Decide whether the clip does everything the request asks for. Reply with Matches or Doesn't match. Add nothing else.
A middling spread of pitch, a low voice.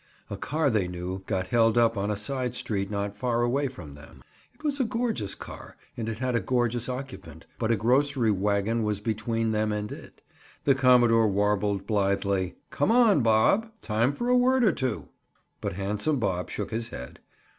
Matches